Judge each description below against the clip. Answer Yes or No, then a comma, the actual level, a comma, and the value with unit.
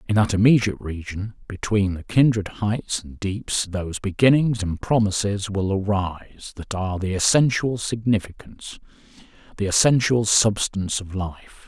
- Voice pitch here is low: Yes, low, 105 Hz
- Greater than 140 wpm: No, slow, 135 wpm